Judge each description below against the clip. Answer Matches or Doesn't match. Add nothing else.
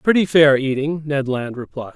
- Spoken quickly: Doesn't match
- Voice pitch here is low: Doesn't match